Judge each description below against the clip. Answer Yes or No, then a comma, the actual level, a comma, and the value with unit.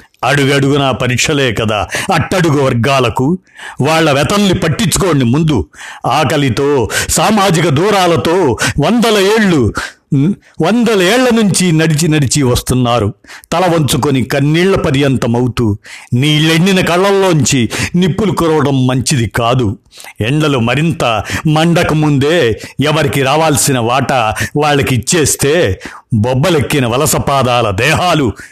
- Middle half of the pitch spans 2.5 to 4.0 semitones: No, average, 4.4 semitones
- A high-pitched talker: No, medium, 145 Hz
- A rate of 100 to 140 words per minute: No, average, 90 wpm